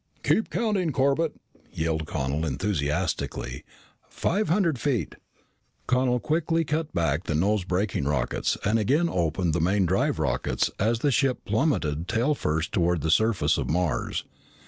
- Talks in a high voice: No, low, 100 Hz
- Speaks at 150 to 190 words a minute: No, average, 140 wpm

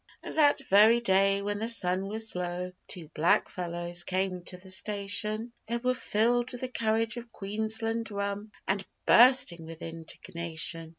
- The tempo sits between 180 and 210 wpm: No, average, 155 wpm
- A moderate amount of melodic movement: Yes, average, 4.0 semitones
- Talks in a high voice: Yes, high, 200 Hz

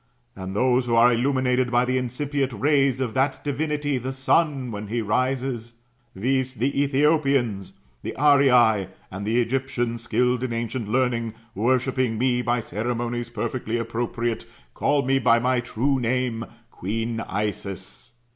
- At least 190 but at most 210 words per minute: No, average, 140 wpm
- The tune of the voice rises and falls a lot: No, narrow, 2.4 semitones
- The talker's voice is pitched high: No, low, 125 Hz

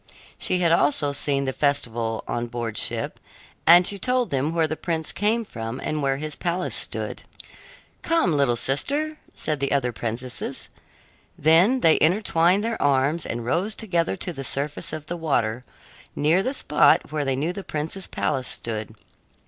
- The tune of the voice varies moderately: Yes, average, 5.0 semitones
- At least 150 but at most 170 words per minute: Yes, average, 165 wpm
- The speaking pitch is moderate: Yes, medium, 150 Hz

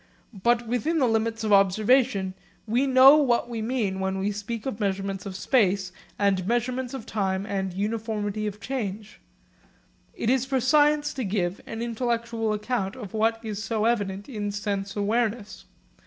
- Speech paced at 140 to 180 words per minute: Yes, average, 160 wpm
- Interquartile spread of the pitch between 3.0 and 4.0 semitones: Yes, average, 3.3 semitones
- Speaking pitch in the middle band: No, high, 220 Hz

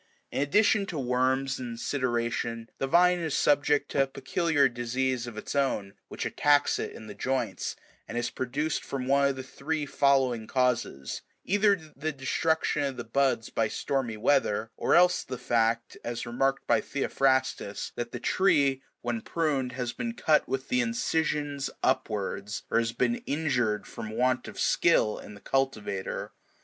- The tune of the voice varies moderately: Yes, average, 3.7 semitones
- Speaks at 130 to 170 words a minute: Yes, average, 165 wpm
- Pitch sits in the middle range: No, low, 130 Hz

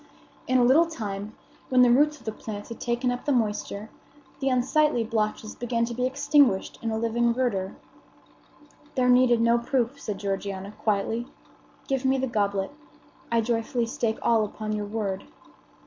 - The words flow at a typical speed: Yes, average, 165 wpm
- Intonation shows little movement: No, average, 3.1 semitones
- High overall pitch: Yes, high, 235 Hz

